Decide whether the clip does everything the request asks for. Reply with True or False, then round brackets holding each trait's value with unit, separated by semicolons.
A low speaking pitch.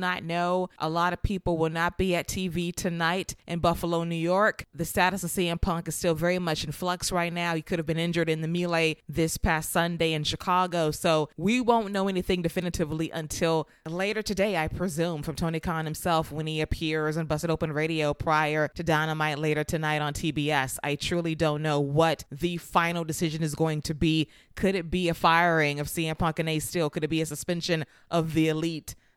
False (165 Hz)